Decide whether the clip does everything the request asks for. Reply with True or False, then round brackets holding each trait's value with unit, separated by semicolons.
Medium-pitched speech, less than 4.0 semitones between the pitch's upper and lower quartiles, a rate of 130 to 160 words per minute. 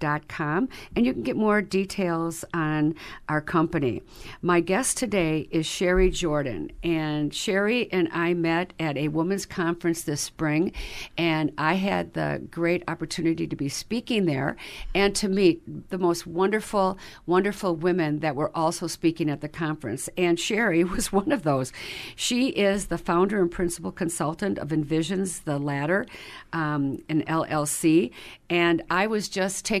True (170 Hz; 3.4 semitones; 155 wpm)